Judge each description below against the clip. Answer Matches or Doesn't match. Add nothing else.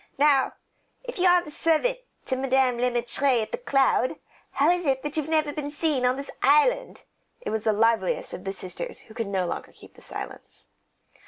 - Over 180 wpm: Matches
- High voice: Matches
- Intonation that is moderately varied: Matches